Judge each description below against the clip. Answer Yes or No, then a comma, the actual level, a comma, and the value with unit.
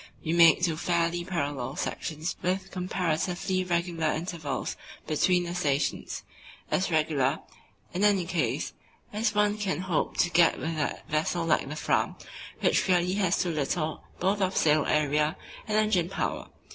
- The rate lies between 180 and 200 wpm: No, average, 150 wpm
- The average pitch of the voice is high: No, medium, 170 Hz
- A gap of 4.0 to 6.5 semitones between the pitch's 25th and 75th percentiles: No, average, 3.1 semitones